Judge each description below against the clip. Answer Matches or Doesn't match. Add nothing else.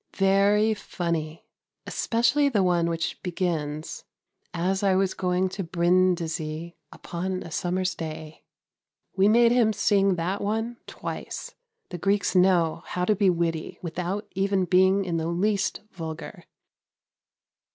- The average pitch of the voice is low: Doesn't match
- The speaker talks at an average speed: Doesn't match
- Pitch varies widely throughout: Doesn't match